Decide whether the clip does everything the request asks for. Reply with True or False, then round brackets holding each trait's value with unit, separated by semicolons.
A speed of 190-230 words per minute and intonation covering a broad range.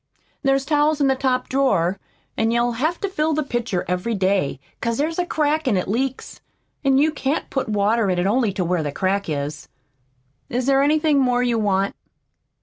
True (195 wpm; 6.1 semitones)